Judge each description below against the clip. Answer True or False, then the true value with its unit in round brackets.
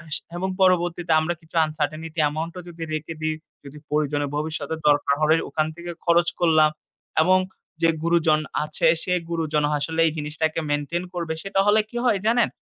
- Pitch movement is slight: True (2.1 semitones)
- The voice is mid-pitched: True (160 Hz)